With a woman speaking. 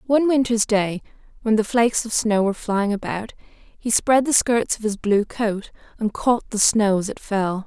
Yes: female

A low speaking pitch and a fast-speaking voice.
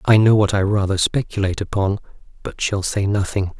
No: low, 100 Hz; average, 185 wpm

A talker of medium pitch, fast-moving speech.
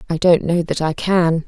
Yes: medium, 170 Hz; fast, 245 wpm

